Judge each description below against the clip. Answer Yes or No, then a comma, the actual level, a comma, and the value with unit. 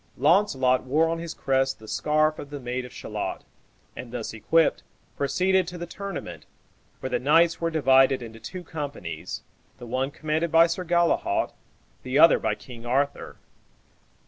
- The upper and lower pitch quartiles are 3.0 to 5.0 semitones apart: Yes, average, 4.6 semitones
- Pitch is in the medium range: Yes, medium, 145 Hz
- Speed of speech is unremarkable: Yes, average, 160 wpm